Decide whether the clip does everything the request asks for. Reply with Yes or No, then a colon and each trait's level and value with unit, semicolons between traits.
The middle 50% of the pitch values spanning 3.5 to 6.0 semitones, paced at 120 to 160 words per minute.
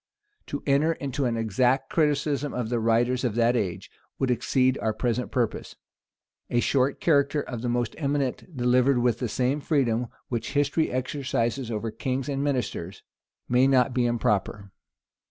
No: average, 2.8 semitones; average, 155 wpm